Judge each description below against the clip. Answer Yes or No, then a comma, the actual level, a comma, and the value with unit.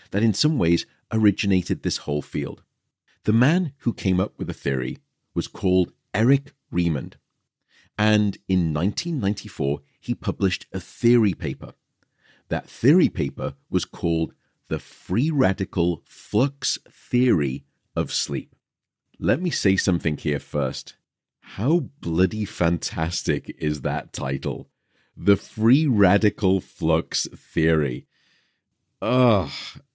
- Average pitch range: No, wide, 5.7 semitones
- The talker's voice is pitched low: Yes, low, 100 Hz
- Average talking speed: No, slow, 115 wpm